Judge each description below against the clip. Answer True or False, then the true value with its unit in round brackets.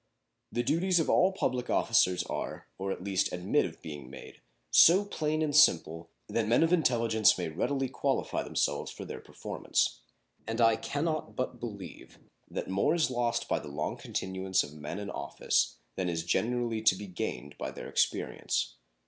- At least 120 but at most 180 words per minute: True (175 wpm)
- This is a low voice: True (110 Hz)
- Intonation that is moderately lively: False (7.0 semitones)